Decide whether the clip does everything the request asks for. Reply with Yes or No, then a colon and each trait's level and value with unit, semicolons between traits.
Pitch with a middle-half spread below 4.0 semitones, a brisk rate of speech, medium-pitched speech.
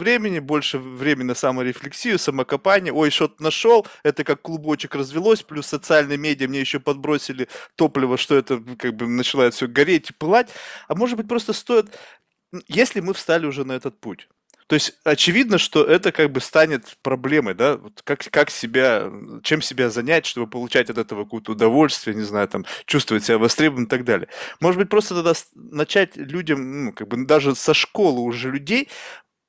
No: average, 4.4 semitones; fast, 175 wpm; medium, 150 Hz